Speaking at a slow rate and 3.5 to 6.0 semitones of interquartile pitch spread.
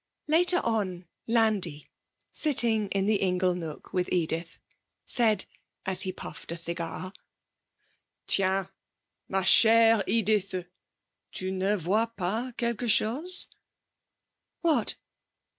Yes: slow, 105 wpm; average, 3.8 semitones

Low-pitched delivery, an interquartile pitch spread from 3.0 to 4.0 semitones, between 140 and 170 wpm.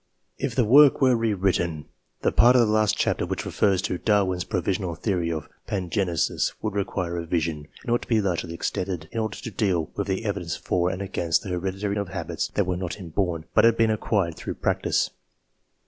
No: very low, 95 Hz; average, 3.7 semitones; average, 200 wpm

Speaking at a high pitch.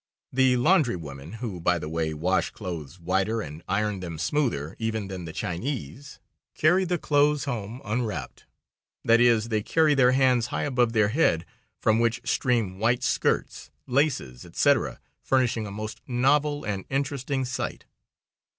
No: low, 115 Hz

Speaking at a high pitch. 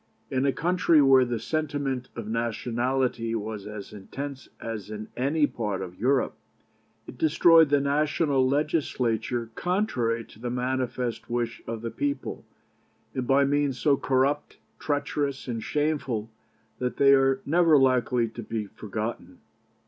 No: low, 130 Hz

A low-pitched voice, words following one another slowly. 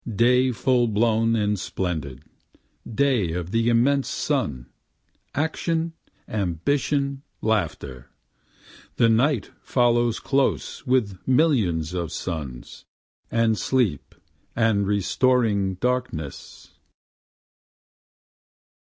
Yes: low, 115 Hz; slow, 80 wpm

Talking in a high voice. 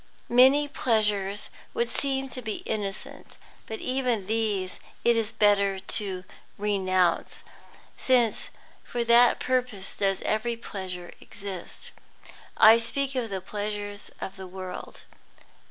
Yes: high, 210 Hz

